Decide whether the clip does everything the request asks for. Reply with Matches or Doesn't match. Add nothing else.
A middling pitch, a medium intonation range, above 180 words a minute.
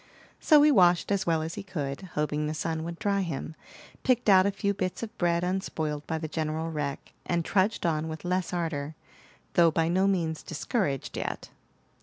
Matches